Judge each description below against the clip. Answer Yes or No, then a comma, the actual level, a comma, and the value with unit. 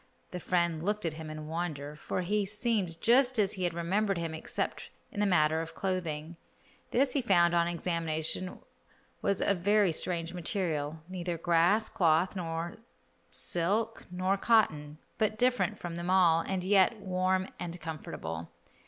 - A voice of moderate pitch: Yes, medium, 180 Hz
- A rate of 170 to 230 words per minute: No, average, 155 wpm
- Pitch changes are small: No, average, 3.4 semitones